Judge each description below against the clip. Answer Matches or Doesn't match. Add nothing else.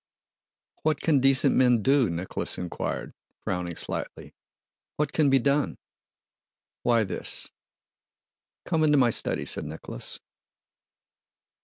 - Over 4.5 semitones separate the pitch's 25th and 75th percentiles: Matches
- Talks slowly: Matches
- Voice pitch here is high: Doesn't match